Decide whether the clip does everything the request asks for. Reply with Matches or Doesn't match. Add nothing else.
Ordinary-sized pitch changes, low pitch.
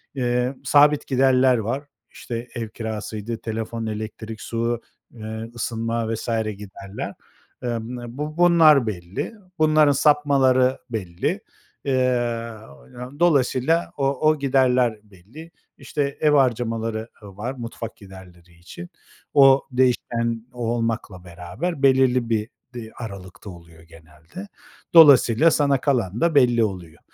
Matches